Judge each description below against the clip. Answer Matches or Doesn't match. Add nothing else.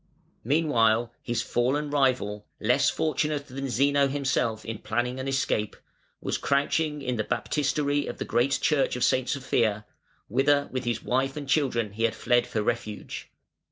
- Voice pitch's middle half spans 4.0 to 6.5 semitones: Doesn't match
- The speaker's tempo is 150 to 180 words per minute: Matches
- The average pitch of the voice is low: Matches